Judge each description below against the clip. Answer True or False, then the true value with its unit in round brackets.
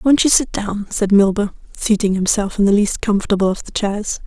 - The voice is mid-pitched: False (205 Hz)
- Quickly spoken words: True (210 wpm)